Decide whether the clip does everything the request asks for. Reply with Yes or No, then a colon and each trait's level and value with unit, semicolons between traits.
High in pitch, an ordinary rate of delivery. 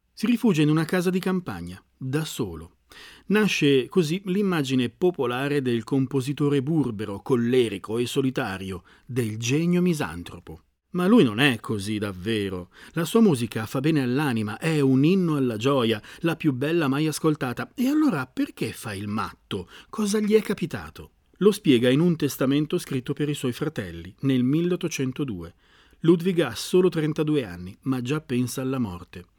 No: low, 135 Hz; average, 155 wpm